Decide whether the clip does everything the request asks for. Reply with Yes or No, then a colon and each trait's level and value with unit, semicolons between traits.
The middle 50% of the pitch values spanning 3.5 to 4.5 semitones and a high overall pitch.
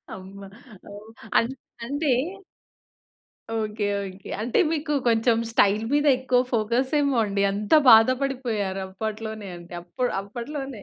Yes: average, 4.1 semitones; high, 225 Hz